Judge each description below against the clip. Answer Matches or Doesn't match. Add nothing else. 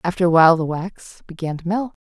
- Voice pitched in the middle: Matches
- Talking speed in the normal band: Doesn't match